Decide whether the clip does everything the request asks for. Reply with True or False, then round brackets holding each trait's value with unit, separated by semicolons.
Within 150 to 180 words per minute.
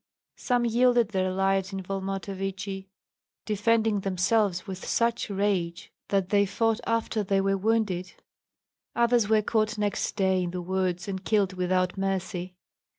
False (140 wpm)